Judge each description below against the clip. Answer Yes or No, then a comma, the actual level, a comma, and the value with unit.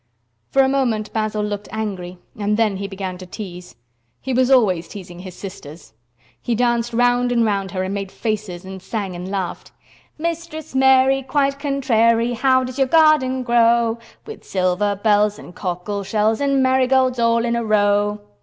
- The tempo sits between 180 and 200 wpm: No, average, 170 wpm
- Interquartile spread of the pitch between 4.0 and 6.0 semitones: Yes, average, 4.6 semitones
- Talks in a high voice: Yes, high, 220 Hz